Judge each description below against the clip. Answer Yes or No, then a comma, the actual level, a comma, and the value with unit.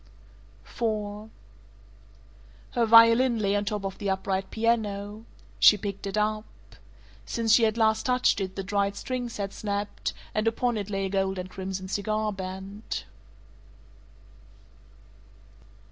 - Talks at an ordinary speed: No, slow, 130 wpm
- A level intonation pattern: Yes, narrow, 2.2 semitones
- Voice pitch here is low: No, high, 205 Hz